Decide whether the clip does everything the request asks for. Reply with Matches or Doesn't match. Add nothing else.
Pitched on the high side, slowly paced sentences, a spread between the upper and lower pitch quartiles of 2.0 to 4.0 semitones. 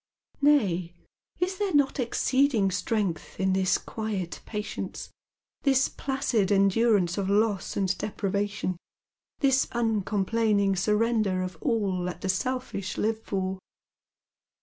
Matches